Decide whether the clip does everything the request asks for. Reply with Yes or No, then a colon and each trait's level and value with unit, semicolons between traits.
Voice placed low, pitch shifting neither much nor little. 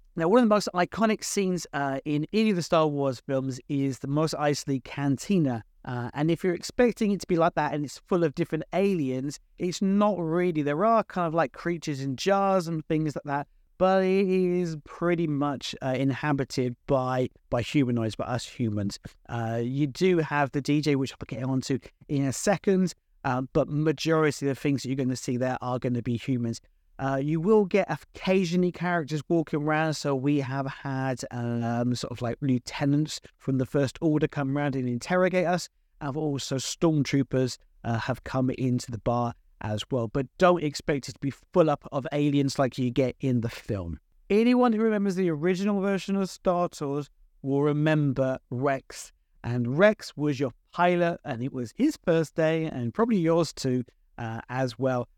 No: medium, 145 Hz; average, 4.9 semitones